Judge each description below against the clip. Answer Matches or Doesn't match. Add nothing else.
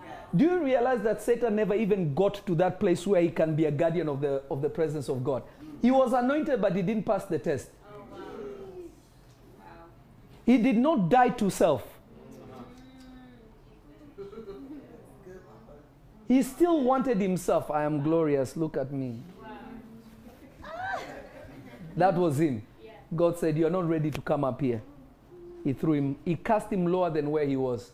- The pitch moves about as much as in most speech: Doesn't match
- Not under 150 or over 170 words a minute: Matches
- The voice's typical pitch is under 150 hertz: Doesn't match